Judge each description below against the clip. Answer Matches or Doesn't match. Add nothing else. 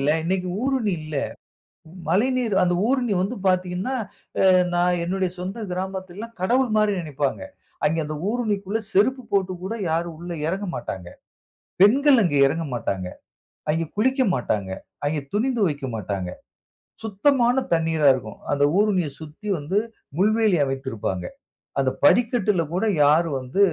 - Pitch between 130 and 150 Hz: Doesn't match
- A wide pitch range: Matches